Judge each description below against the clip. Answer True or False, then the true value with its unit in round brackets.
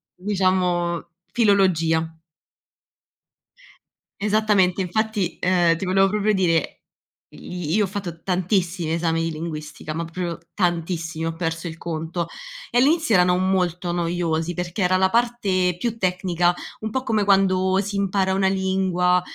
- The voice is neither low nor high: True (180 Hz)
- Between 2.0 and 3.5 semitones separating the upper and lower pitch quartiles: True (2.5 semitones)